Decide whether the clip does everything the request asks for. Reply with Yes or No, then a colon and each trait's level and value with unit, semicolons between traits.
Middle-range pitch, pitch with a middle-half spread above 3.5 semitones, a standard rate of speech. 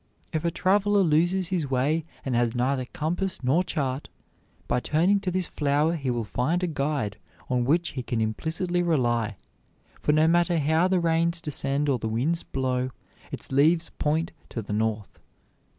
Yes: medium, 150 Hz; average, 5.1 semitones; average, 170 wpm